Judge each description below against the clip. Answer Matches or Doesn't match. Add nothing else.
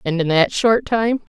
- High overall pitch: Matches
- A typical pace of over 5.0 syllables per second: Doesn't match